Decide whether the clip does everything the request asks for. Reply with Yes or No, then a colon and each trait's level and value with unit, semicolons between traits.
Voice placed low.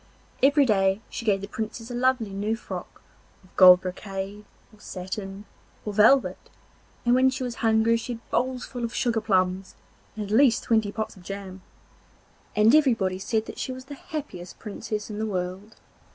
No: high, 215 Hz